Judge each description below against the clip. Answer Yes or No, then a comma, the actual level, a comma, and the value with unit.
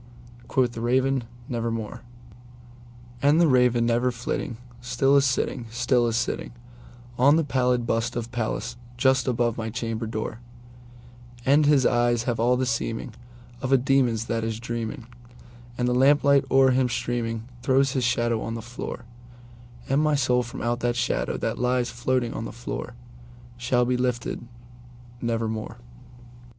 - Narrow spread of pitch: Yes, narrow, 1.1 semitones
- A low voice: Yes, low, 120 Hz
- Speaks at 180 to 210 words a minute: No, average, 140 wpm